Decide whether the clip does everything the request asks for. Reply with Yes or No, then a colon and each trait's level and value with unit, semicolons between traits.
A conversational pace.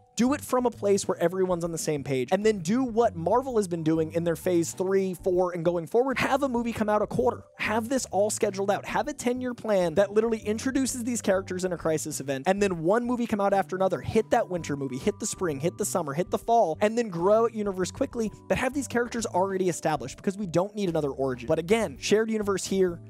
No: fast, 250 wpm